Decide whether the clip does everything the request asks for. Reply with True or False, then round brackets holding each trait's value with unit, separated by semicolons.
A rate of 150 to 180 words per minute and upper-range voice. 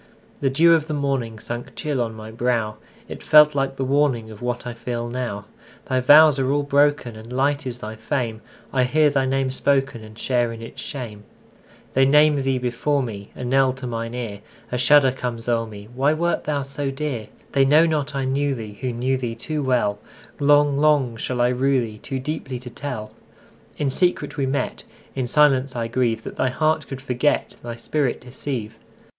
False (160 wpm; 130 Hz)